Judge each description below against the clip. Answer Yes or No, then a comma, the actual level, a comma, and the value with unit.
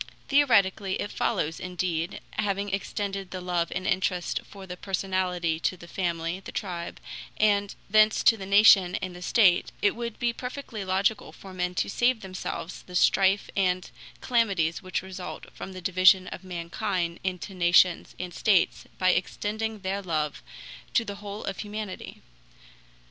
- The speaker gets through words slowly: No, average, 155 wpm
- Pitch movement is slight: Yes, narrow, 2.2 semitones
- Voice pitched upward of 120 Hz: Yes, high, 190 Hz